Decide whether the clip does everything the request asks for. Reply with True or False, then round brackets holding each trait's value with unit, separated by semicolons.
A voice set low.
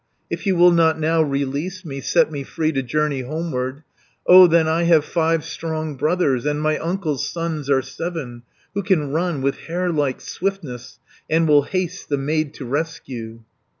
False (155 Hz)